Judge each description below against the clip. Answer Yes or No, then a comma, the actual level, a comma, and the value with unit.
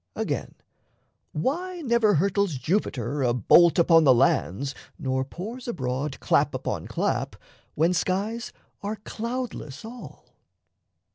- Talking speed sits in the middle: No, slow, 115 wpm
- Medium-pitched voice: Yes, medium, 175 Hz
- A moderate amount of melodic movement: No, wide, 8.6 semitones